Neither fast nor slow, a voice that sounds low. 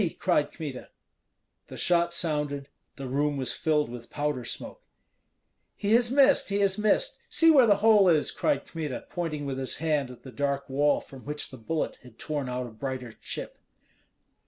No: average, 180 wpm; medium, 150 Hz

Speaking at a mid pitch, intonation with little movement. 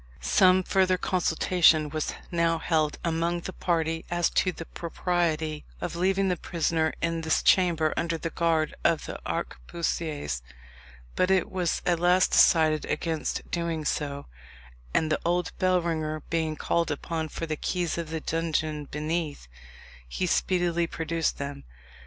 Yes: medium, 165 Hz; narrow, 1.9 semitones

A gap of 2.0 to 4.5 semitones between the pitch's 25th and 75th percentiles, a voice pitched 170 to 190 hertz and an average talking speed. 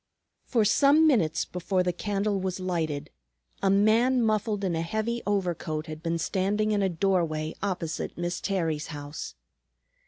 Yes: average, 4.1 semitones; medium, 185 Hz; average, 150 wpm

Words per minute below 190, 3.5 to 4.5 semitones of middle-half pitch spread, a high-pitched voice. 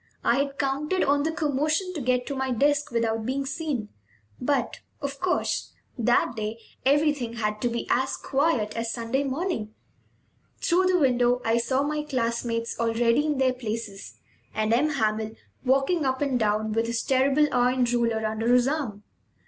Yes: average, 165 wpm; average, 3.8 semitones; very high, 255 Hz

